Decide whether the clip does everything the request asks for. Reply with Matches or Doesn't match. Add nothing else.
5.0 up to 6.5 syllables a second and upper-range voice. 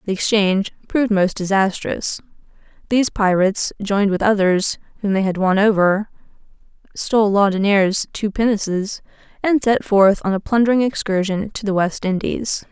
Matches